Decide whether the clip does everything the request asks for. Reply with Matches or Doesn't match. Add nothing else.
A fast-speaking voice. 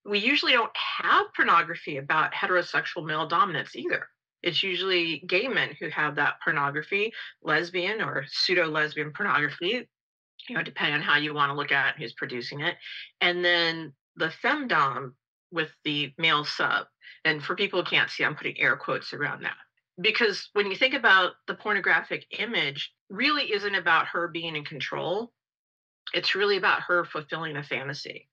Doesn't match